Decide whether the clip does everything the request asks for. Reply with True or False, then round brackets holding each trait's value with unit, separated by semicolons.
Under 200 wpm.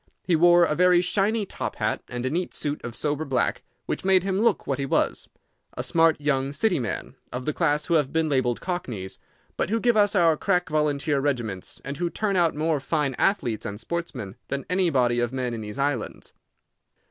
False (205 wpm)